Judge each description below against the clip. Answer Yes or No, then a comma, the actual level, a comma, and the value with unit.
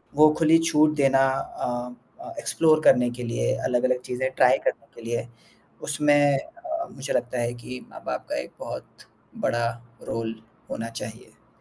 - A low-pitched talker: Yes, low, 130 Hz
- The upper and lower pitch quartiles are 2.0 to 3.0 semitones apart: No, average, 4.1 semitones